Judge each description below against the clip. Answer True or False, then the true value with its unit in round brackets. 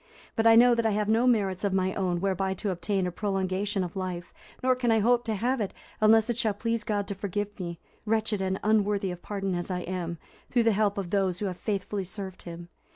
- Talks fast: True (235 wpm)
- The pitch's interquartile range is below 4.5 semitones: True (2.8 semitones)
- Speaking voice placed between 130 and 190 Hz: False (200 Hz)